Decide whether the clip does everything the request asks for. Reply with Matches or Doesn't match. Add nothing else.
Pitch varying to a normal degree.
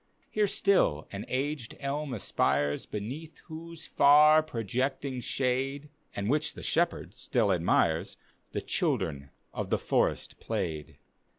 Doesn't match